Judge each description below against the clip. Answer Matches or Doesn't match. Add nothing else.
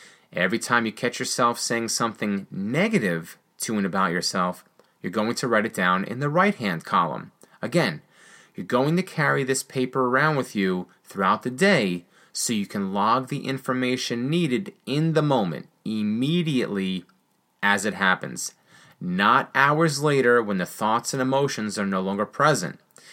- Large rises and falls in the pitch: Matches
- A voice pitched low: Matches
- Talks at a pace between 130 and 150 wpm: Doesn't match